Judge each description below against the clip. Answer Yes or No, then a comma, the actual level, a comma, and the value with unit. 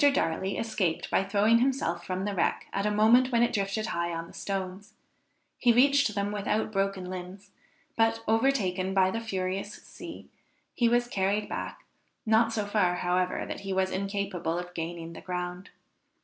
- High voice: Yes, high, 195 Hz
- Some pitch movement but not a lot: Yes, average, 3.2 semitones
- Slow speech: No, average, 170 wpm